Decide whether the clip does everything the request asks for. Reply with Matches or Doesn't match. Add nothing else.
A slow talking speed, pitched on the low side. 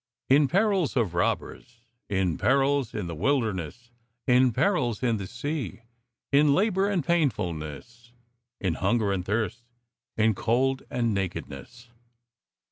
Matches